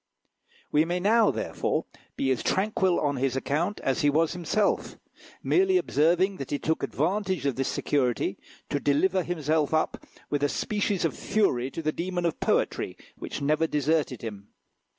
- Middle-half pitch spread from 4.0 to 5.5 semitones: Yes, average, 4.7 semitones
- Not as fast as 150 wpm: No, average, 165 wpm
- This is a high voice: No, medium, 160 Hz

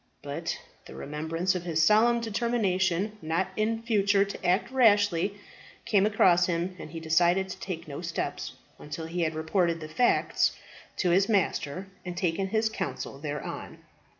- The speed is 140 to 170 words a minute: Yes, average, 155 wpm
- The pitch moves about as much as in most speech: Yes, average, 3.9 semitones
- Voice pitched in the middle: Yes, medium, 180 Hz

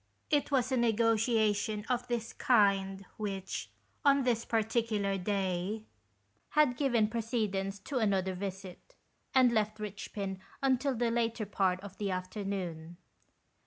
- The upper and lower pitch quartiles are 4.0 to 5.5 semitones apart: No, average, 3.4 semitones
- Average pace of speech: No, slow, 125 wpm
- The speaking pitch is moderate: No, high, 215 Hz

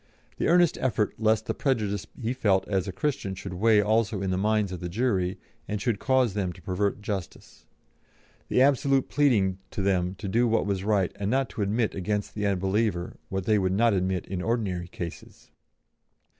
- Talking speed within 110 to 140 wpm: No, average, 190 wpm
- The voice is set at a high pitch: No, low, 100 Hz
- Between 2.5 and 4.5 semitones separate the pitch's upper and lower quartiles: Yes, average, 3.2 semitones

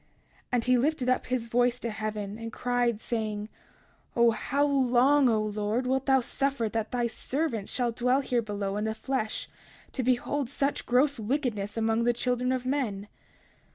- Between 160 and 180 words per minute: Yes, average, 175 wpm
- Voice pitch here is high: Yes, high, 240 Hz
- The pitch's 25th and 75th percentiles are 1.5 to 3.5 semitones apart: Yes, average, 2.9 semitones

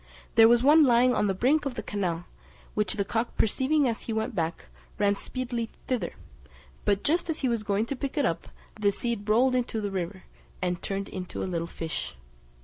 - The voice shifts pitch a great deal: No, average, 4.3 semitones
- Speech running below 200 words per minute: No, fast, 205 wpm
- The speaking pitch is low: No, high, 225 Hz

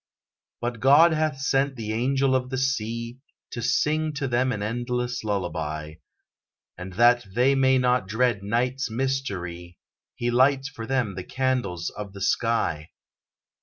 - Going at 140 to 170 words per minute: Yes, average, 145 wpm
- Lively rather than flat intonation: No, average, 4.1 semitones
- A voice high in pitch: No, low, 120 Hz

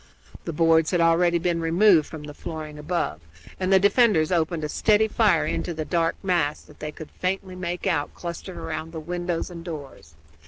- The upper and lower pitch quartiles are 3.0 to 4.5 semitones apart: No, narrow, 2.5 semitones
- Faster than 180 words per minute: Yes, average, 190 wpm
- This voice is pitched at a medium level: Yes, medium, 170 Hz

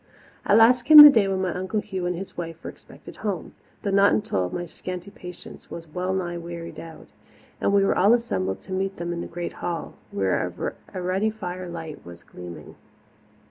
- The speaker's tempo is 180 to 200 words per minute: Yes, average, 195 wpm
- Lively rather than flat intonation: No, average, 2.8 semitones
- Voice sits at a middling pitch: Yes, medium, 180 Hz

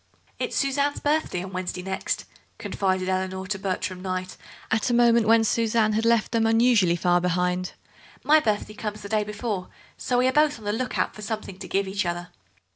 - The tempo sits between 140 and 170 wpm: No, average, 200 wpm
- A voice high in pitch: Yes, high, 210 Hz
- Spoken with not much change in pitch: No, average, 3.7 semitones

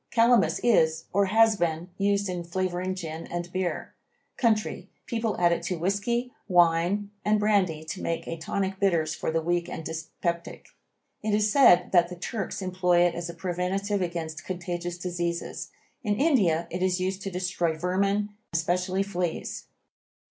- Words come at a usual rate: Yes, average, 160 wpm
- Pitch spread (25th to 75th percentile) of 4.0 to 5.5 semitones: No, average, 2.8 semitones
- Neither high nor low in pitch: Yes, medium, 180 Hz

